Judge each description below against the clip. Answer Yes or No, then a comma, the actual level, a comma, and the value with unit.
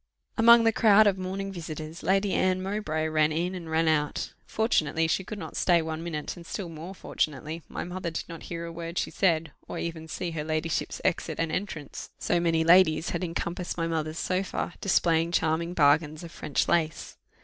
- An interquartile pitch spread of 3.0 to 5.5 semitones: No, narrow, 2.6 semitones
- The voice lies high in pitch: No, medium, 165 Hz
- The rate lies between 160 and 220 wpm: Yes, average, 195 wpm